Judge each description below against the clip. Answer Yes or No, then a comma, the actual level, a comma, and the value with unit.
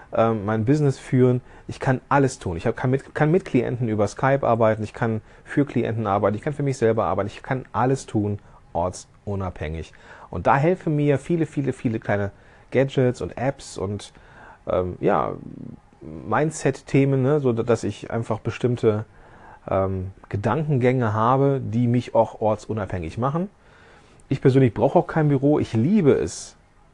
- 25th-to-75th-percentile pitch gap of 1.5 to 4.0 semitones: No, average, 4.5 semitones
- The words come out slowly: No, average, 155 wpm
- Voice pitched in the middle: No, low, 120 Hz